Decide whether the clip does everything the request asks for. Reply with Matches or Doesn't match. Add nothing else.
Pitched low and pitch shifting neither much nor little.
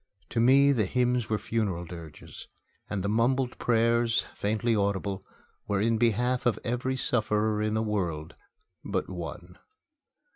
Matches